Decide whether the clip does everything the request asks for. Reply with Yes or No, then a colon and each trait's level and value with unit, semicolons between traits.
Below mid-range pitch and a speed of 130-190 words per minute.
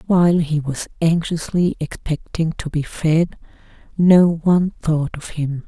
No: medium, 160 Hz; average, 140 wpm